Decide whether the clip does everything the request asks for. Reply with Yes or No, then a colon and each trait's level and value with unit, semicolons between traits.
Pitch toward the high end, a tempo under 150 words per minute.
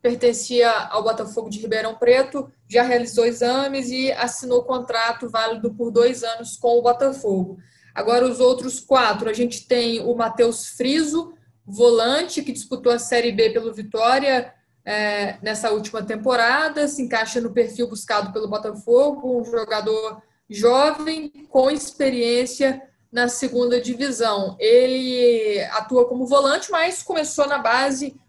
Yes: high, 240 Hz; average, 135 wpm